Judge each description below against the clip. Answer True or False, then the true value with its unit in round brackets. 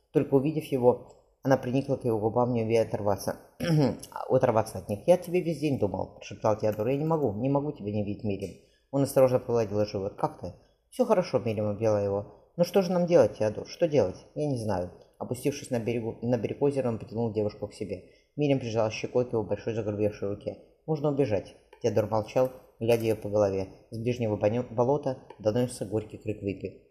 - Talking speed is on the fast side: True (190 wpm)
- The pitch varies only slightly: False (4.3 semitones)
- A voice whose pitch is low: True (115 Hz)